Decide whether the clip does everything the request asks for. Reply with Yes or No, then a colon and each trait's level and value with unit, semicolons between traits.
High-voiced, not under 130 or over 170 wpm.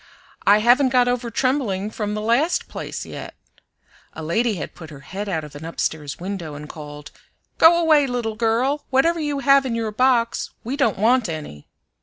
No: high, 225 Hz; average, 185 wpm